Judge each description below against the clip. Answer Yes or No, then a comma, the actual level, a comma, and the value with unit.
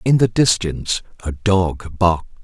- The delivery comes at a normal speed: Yes, average, 150 wpm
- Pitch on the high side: No, very low, 90 Hz